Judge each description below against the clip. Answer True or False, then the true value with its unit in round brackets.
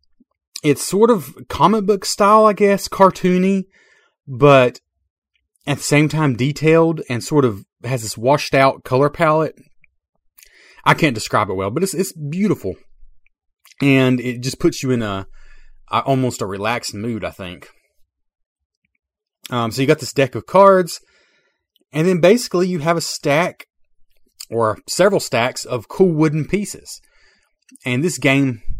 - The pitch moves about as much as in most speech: False (6.5 semitones)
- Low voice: False (145 Hz)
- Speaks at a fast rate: False (150 wpm)